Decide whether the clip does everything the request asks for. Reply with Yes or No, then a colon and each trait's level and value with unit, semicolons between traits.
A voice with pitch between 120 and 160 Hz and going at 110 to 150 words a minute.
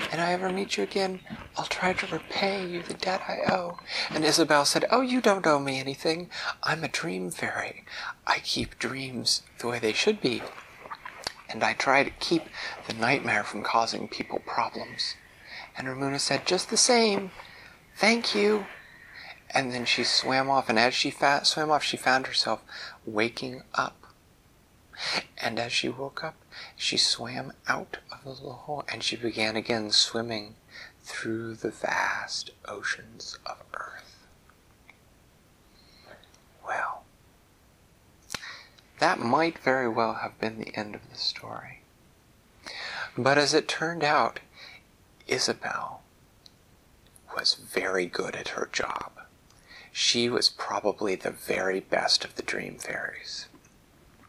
Yes: low, 135 Hz; average, 140 wpm